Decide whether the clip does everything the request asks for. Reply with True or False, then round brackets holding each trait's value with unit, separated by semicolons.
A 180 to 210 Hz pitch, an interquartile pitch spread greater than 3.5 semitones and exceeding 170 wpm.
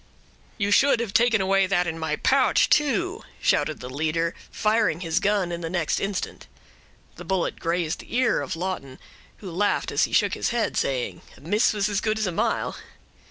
True (190 Hz; 4.5 semitones; 195 wpm)